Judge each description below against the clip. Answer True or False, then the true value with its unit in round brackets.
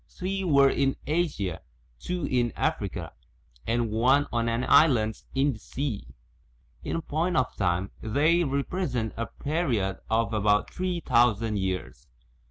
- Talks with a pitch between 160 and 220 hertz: False (125 Hz)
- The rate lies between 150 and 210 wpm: False (135 wpm)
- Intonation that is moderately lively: False (5.8 semitones)